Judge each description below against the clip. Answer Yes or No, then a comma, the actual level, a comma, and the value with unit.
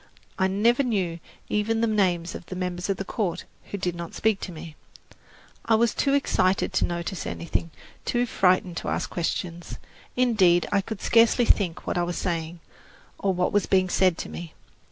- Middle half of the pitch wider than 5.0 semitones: No, average, 3.7 semitones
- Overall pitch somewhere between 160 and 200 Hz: Yes, medium, 185 Hz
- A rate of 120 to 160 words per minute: No, average, 185 wpm